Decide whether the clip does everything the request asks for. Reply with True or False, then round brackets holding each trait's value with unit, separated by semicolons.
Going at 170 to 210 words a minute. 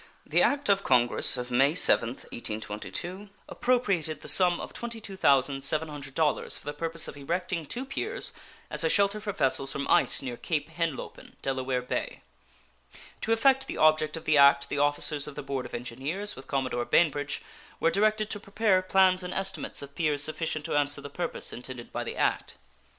True (175 wpm)